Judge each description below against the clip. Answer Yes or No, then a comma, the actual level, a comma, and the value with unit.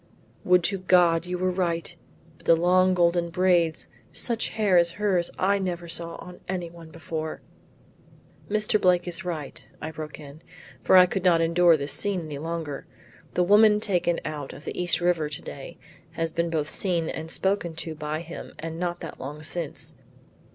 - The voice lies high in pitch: No, medium, 170 Hz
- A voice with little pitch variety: Yes, narrow, 2.1 semitones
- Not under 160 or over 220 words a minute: Yes, average, 180 wpm